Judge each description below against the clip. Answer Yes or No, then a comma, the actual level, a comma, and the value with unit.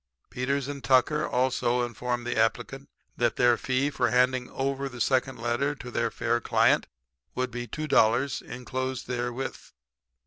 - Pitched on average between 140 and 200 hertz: No, low, 125 Hz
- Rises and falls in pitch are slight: Yes, narrow, 1.8 semitones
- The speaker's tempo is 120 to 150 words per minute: Yes, average, 145 wpm